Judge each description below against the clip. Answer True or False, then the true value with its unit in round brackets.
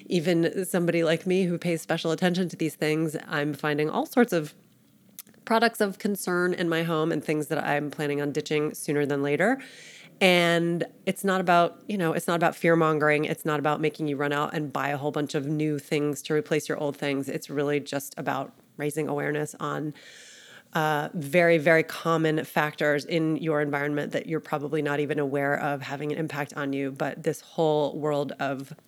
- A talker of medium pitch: True (155 Hz)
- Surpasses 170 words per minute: True (195 wpm)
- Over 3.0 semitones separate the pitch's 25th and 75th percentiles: False (2.5 semitones)